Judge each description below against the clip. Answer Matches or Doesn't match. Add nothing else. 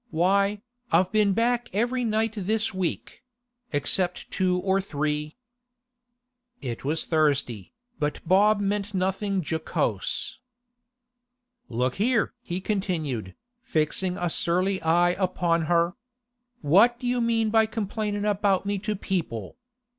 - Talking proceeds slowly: Matches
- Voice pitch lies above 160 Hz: Matches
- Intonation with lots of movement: Doesn't match